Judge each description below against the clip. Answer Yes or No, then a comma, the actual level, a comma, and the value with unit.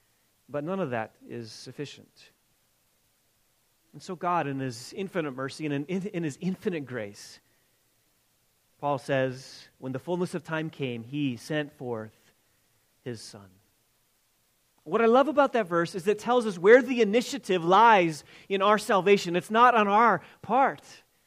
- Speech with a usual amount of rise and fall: No, wide, 7.9 semitones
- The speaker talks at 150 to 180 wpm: Yes, average, 155 wpm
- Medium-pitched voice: Yes, medium, 155 Hz